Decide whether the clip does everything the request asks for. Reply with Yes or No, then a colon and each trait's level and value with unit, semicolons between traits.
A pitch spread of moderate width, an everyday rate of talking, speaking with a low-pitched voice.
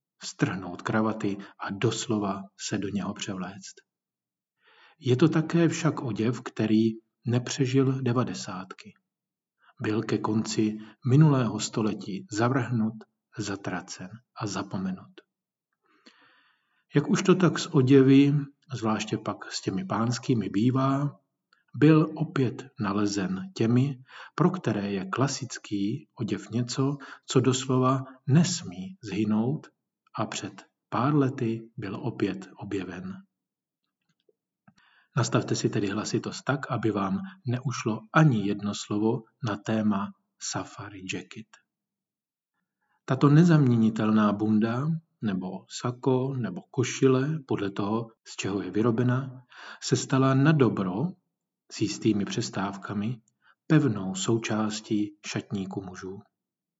No: average, 4.4 semitones; slow, 100 wpm; low, 115 Hz